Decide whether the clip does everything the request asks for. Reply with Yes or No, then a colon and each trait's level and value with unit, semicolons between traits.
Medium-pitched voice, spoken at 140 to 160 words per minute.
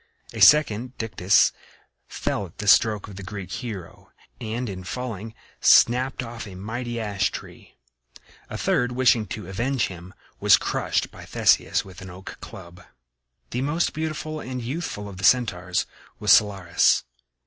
No: low, 110 Hz; average, 150 wpm